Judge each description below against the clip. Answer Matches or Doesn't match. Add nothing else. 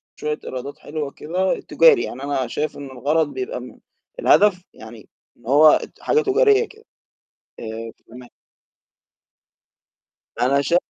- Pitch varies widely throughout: Matches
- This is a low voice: Doesn't match